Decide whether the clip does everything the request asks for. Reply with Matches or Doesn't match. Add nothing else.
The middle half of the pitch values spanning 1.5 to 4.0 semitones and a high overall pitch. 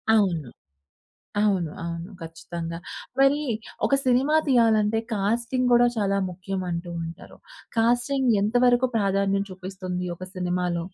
Doesn't match